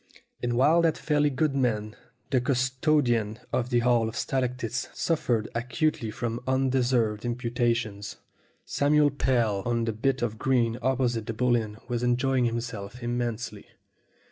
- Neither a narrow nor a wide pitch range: No, narrow, 2.3 semitones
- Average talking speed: Yes, average, 145 wpm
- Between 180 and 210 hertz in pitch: No, low, 120 Hz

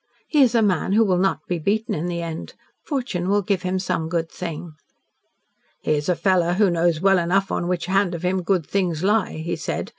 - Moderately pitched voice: Yes, medium, 180 Hz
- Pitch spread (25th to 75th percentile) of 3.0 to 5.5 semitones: No, narrow, 2.6 semitones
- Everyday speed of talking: No, fast, 220 wpm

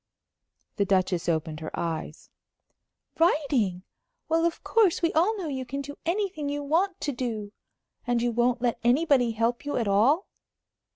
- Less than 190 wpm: Yes, average, 160 wpm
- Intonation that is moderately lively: No, wide, 7.1 semitones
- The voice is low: No, very high, 255 Hz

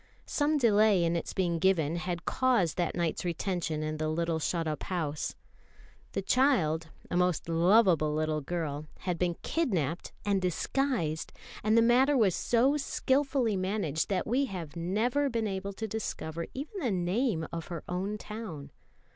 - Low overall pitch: No, medium, 185 Hz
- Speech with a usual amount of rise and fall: No, wide, 5.7 semitones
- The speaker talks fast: No, average, 160 wpm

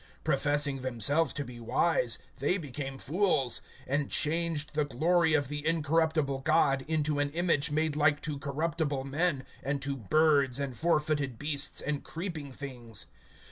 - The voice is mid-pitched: Yes, medium, 145 Hz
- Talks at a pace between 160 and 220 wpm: No, average, 145 wpm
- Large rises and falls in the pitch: No, narrow, 2.6 semitones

